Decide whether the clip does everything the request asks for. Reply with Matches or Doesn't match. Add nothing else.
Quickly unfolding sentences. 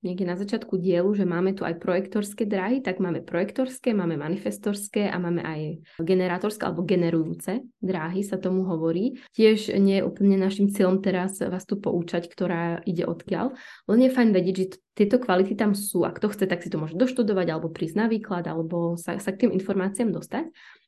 Matches